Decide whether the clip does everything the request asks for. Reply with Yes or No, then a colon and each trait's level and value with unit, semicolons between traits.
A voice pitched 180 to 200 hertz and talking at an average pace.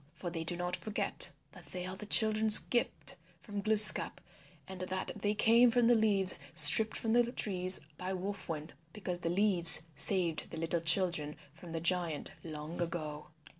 Yes: medium, 185 Hz; average, 170 wpm